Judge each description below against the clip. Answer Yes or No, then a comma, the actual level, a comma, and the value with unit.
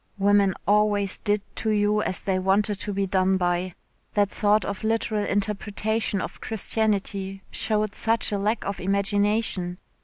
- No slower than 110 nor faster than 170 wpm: Yes, average, 150 wpm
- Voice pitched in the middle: No, high, 205 Hz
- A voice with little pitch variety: Yes, narrow, 1.5 semitones